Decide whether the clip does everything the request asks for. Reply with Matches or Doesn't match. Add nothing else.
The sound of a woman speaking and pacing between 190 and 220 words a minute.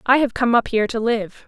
Doesn't match